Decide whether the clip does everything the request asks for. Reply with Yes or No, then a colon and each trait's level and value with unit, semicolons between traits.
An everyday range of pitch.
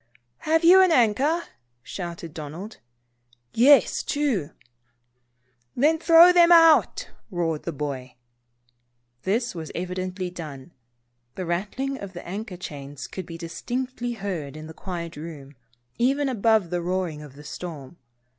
No: wide, 7.8 semitones